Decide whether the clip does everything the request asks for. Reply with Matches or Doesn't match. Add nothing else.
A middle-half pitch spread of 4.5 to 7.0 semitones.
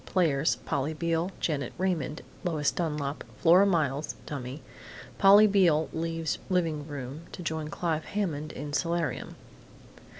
Doesn't match